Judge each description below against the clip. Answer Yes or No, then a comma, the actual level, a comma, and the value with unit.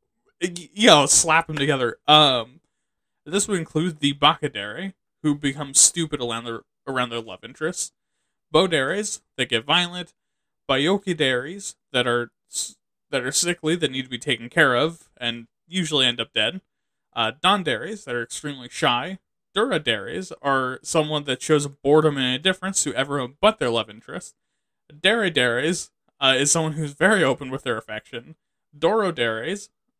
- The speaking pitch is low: No, medium, 150 Hz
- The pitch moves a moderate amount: No, wide, 5.7 semitones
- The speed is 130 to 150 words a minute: Yes, average, 145 wpm